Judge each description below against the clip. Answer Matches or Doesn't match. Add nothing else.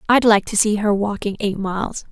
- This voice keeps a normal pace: Doesn't match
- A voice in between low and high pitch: Doesn't match